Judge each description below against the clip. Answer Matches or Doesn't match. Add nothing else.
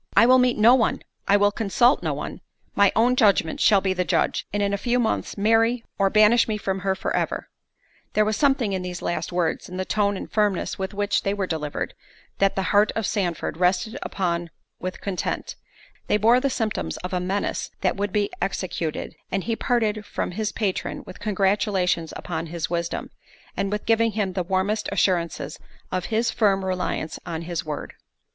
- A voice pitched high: Matches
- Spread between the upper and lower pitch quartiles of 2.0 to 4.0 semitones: Matches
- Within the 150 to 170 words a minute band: Doesn't match